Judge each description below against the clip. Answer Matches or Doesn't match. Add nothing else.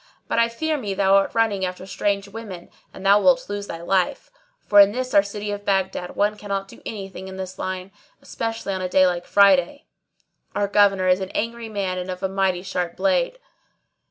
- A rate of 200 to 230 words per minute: Matches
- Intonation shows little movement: Matches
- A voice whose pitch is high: Matches